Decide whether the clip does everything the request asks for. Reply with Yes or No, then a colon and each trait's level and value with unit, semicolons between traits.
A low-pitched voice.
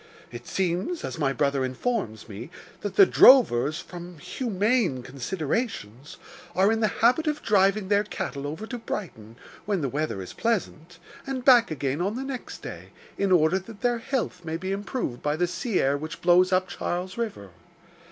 No: medium, 185 Hz